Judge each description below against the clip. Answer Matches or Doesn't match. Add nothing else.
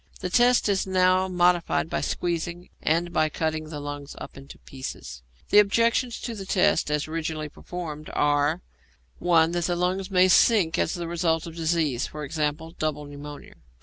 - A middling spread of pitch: Matches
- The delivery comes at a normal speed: Matches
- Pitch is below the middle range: Doesn't match